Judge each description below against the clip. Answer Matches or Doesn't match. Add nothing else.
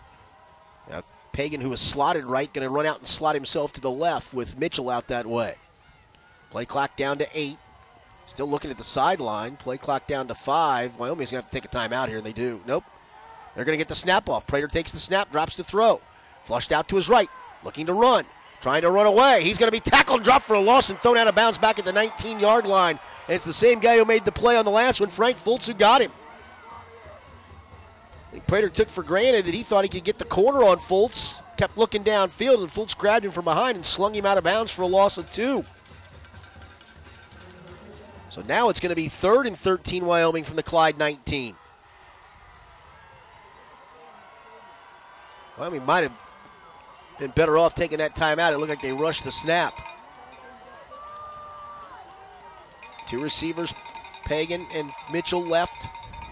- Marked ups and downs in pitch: Matches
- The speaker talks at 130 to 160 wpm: Doesn't match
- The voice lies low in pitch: Doesn't match